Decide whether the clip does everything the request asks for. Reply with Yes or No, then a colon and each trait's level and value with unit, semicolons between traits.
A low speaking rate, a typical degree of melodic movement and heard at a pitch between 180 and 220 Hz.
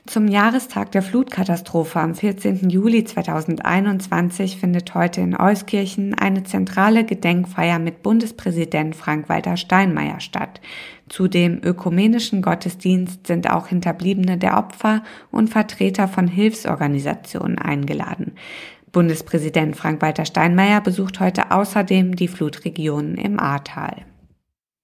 Yes: slow, 105 wpm; average, 3.3 semitones; medium, 185 Hz